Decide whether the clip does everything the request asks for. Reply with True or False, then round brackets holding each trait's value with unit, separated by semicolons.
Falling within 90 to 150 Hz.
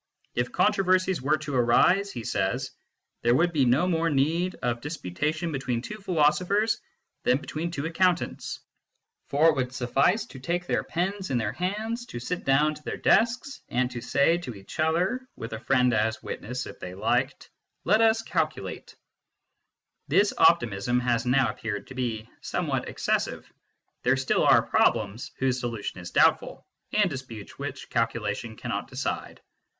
True (140 Hz)